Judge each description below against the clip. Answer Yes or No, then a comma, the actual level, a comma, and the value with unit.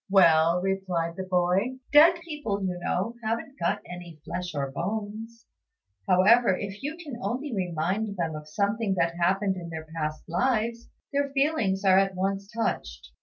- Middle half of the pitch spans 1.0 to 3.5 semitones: No, average, 4.7 semitones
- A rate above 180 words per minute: No, average, 160 wpm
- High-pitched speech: Yes, high, 195 Hz